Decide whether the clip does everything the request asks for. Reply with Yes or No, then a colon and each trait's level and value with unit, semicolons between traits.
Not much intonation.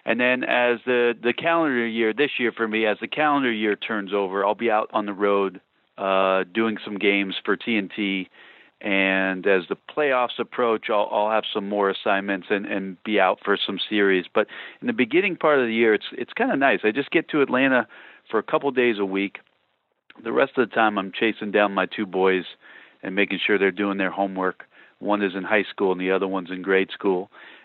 No: average, 3.1 semitones